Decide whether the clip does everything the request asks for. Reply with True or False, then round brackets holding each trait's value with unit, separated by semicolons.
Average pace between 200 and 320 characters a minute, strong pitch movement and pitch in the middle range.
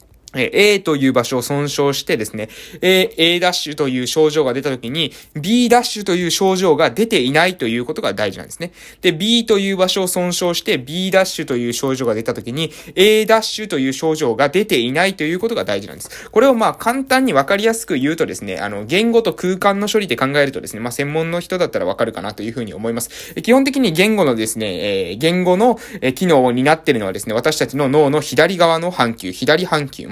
False (410 characters per minute; 6.5 semitones; 165 Hz)